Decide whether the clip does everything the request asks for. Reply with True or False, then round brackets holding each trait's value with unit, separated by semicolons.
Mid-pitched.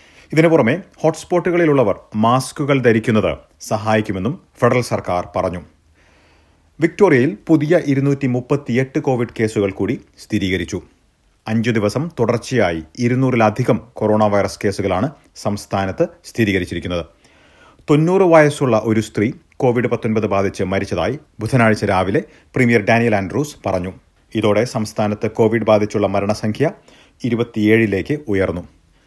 False (110 Hz)